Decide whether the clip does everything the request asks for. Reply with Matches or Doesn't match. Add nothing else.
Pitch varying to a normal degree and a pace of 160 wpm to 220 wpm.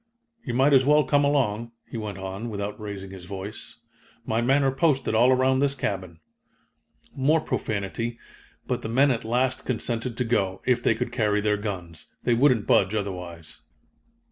Matches